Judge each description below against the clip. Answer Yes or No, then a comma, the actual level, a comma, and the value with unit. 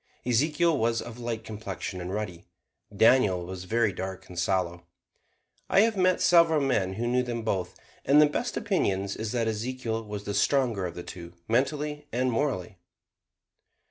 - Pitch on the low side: Yes, low, 115 Hz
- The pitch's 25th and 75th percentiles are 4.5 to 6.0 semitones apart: Yes, wide, 5.5 semitones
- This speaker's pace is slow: No, average, 165 wpm